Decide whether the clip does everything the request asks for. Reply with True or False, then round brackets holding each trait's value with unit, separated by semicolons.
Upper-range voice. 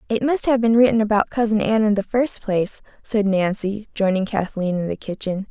True (210 Hz)